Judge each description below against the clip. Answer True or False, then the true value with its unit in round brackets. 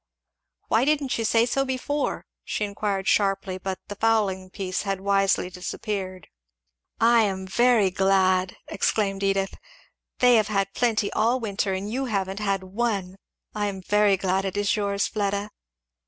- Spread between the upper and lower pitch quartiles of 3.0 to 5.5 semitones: False (2.4 semitones)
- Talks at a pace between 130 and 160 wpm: True (155 wpm)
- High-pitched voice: True (200 Hz)